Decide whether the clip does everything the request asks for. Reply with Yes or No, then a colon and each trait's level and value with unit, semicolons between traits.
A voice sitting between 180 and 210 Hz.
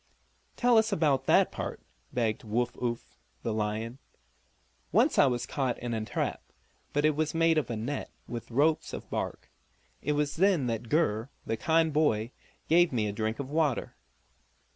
No: low, 130 Hz